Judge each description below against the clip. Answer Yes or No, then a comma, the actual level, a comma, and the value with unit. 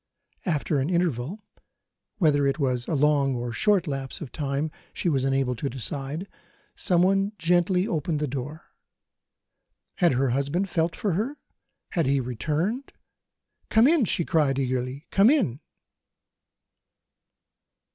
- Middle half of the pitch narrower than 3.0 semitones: No, average, 4.8 semitones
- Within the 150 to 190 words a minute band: No, slow, 135 wpm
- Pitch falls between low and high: Yes, medium, 150 Hz